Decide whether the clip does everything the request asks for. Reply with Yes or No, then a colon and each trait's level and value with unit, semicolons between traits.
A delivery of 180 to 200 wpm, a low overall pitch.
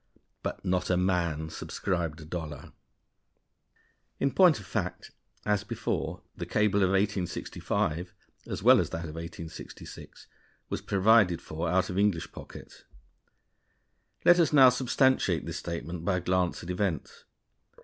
No: average, 140 wpm; very low, 90 Hz